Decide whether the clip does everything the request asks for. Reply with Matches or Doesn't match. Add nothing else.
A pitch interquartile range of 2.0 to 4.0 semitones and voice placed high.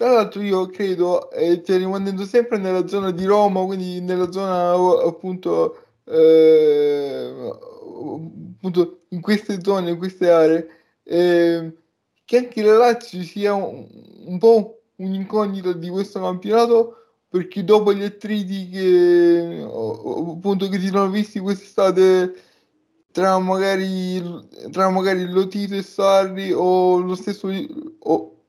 Matches